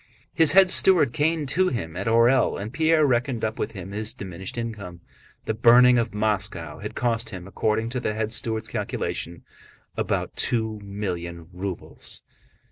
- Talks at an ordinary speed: Yes, average, 160 wpm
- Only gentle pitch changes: No, average, 4.1 semitones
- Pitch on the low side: Yes, low, 110 Hz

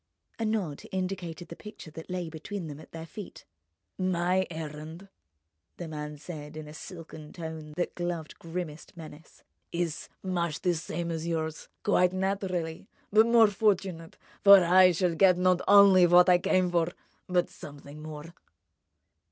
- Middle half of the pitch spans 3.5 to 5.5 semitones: No, narrow, 2.6 semitones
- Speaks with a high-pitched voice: No, medium, 175 Hz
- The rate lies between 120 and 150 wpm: Yes, average, 145 wpm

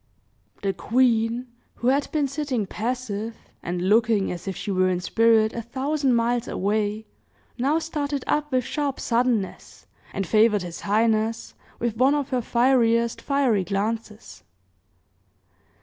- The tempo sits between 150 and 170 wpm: No, slow, 135 wpm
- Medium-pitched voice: No, high, 230 Hz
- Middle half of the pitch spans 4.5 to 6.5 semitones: No, average, 3.6 semitones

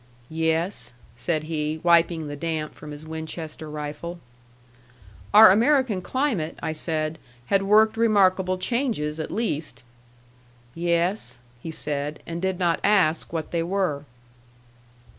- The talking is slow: Yes, slow, 125 wpm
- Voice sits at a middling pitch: Yes, medium, 165 Hz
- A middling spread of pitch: Yes, average, 3.8 semitones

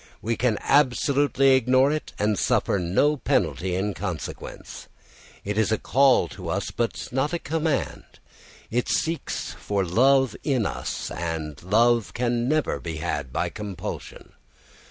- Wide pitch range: Yes, wide, 6.1 semitones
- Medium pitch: No, low, 115 Hz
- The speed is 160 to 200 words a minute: No, average, 140 wpm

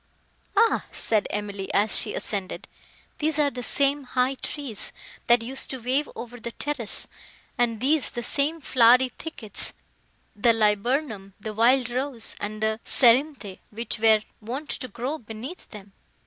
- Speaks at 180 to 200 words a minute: No, average, 140 wpm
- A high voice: Yes, high, 240 Hz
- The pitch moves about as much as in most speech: Yes, average, 4.0 semitones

